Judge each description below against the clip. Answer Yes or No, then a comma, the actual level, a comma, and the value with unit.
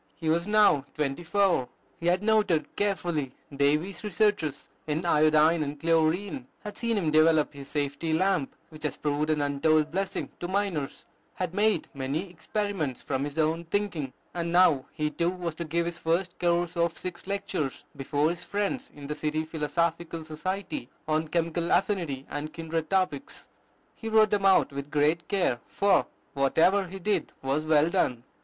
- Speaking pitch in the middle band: Yes, medium, 165 Hz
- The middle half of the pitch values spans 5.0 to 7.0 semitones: No, average, 3.8 semitones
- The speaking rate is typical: Yes, average, 165 wpm